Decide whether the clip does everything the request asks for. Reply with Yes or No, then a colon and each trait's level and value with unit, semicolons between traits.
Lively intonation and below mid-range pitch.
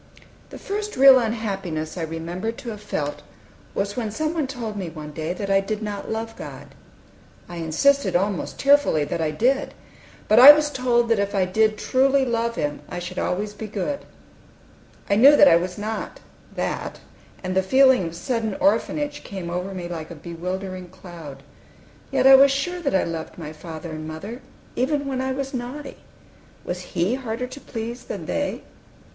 No: wide, 6.7 semitones; high, 210 Hz